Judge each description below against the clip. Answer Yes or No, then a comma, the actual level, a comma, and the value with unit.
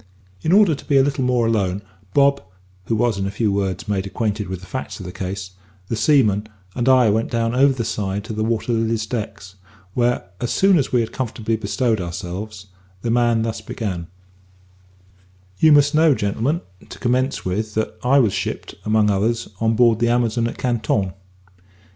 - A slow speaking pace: No, average, 190 wpm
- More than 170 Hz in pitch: No, low, 115 Hz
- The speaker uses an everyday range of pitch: Yes, average, 3.4 semitones